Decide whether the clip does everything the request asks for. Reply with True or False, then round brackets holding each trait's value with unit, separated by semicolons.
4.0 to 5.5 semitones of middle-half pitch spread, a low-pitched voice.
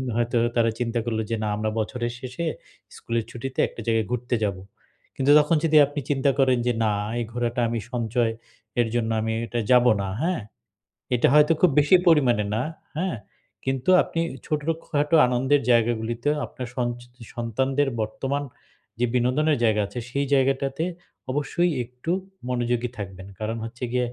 False (3.3 semitones; 125 Hz)